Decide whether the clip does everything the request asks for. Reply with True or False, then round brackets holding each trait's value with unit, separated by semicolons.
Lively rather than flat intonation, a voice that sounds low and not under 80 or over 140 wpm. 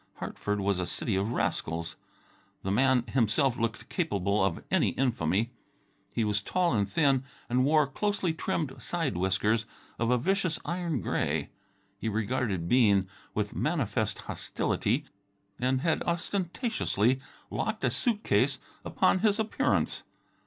True (7.7 semitones; 125 Hz; 135 wpm)